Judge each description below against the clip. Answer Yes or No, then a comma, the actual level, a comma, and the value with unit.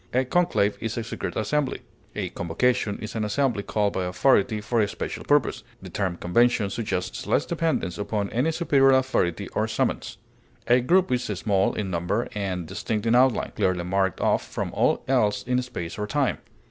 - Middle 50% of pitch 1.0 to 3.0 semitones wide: No, average, 4.4 semitones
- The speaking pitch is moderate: No, low, 110 Hz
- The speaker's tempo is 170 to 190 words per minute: Yes, average, 180 wpm